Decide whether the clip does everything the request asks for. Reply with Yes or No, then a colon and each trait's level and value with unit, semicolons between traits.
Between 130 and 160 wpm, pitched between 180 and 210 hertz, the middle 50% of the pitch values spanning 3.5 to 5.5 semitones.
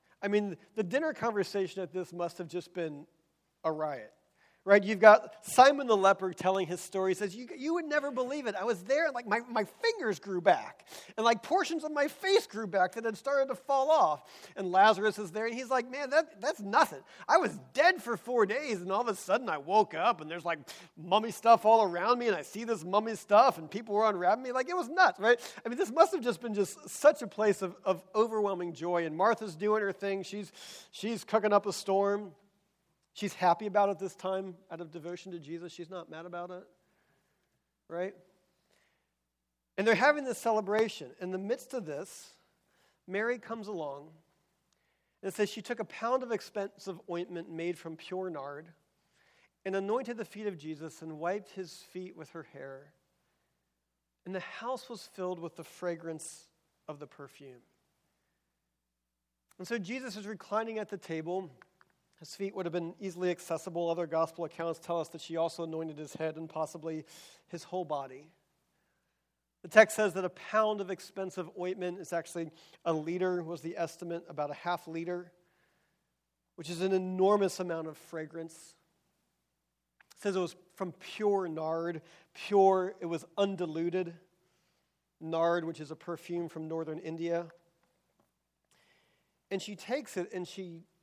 No: average, 185 wpm; medium, 185 Hz; average, 4.3 semitones